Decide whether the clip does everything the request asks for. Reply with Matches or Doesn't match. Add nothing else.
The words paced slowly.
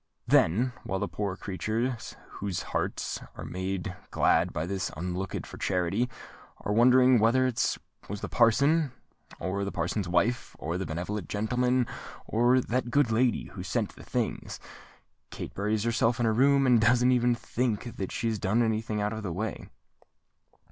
Doesn't match